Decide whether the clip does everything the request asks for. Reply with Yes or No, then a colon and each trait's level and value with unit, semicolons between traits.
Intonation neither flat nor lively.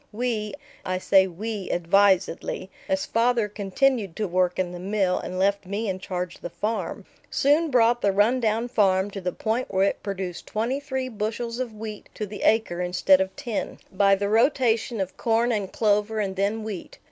Yes: average, 3.2 semitones